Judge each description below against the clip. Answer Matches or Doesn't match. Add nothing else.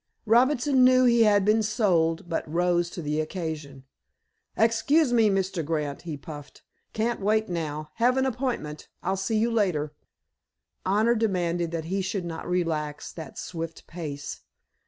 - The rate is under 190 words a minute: Matches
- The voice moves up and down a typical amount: Doesn't match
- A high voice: Doesn't match